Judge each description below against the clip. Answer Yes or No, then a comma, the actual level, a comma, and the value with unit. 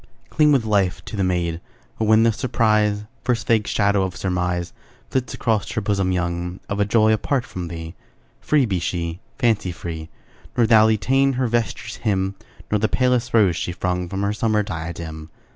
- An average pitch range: Yes, average, 4.0 semitones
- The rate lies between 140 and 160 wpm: No, average, 180 wpm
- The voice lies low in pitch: Yes, low, 100 Hz